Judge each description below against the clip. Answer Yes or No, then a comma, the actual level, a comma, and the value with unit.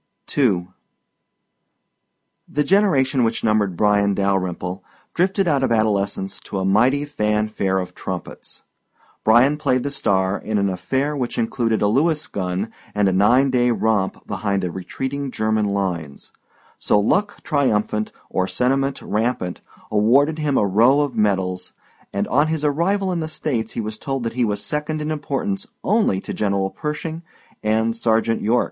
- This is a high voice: No, low, 115 Hz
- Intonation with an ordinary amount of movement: No, wide, 6.0 semitones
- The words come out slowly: No, average, 155 wpm